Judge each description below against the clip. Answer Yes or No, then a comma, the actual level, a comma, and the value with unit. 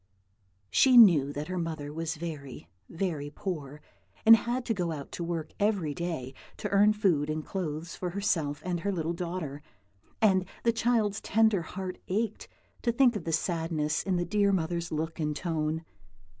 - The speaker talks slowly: No, average, 170 wpm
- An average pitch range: Yes, average, 4.4 semitones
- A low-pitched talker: No, medium, 170 Hz